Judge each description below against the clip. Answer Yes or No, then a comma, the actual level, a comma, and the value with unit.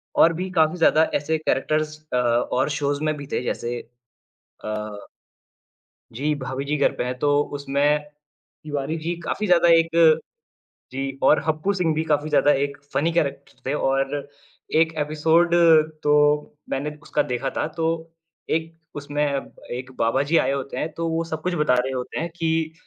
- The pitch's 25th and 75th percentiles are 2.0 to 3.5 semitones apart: Yes, average, 2.9 semitones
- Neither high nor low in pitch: Yes, medium, 150 Hz